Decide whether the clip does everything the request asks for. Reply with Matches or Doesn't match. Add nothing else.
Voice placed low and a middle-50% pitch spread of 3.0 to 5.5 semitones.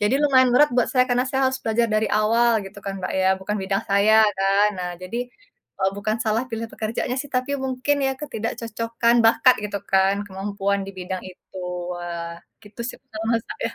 Doesn't match